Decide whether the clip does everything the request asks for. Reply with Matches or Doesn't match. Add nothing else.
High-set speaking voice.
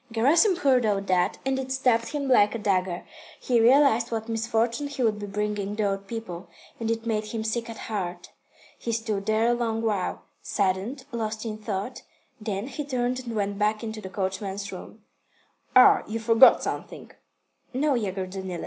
Matches